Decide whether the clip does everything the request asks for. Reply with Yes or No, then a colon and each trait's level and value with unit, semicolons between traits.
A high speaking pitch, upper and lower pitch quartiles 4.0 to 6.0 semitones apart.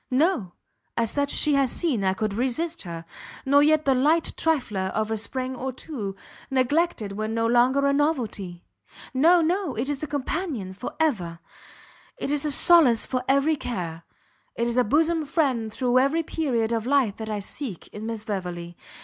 Yes: very high, 255 Hz; wide, 5.4 semitones